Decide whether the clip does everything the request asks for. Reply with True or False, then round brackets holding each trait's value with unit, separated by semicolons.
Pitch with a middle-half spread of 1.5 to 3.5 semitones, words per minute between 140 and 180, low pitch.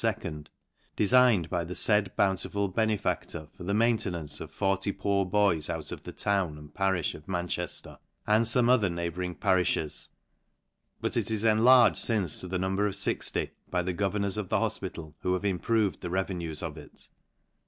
True (3.0 semitones; 175 wpm; 95 Hz)